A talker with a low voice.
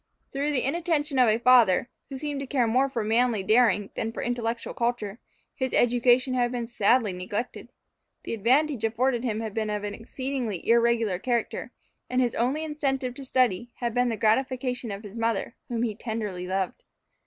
No: high, 240 Hz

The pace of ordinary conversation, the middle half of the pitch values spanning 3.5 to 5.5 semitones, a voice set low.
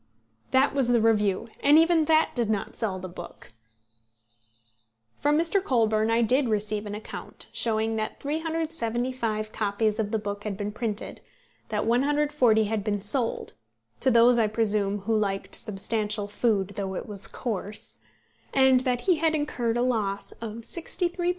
No: average, 165 wpm; average, 3.9 semitones; high, 225 Hz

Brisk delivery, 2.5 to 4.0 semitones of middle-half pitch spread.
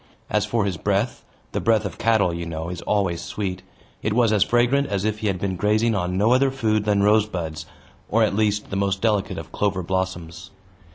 Yes: fast, 210 wpm; average, 2.8 semitones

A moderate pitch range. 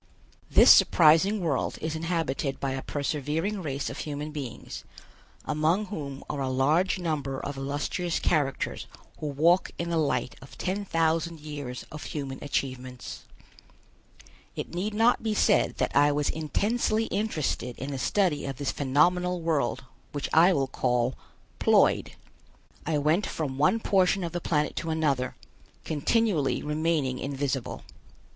Yes: average, 4.0 semitones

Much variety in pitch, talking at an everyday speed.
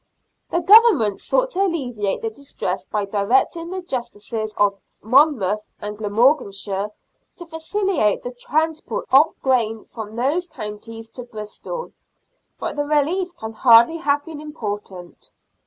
No: wide, 7.3 semitones; slow, 130 wpm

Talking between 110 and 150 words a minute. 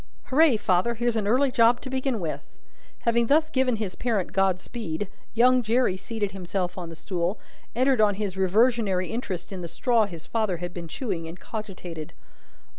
No: average, 180 wpm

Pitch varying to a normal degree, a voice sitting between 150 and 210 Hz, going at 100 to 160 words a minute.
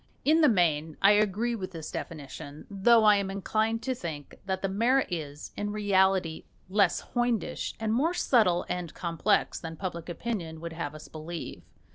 No: average, 4.8 semitones; high, 190 Hz; average, 170 wpm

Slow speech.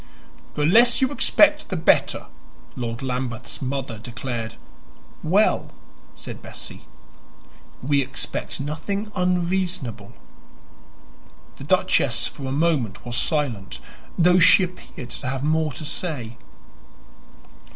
Yes: slow, 110 wpm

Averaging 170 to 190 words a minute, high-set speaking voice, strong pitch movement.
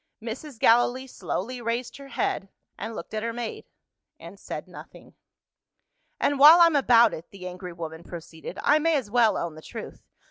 Yes: average, 175 wpm; high, 230 Hz; wide, 6.4 semitones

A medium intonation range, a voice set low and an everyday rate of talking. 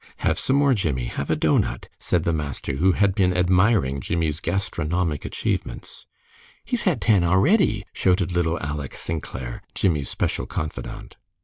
Yes: average, 4.4 semitones; very low, 85 Hz; average, 145 wpm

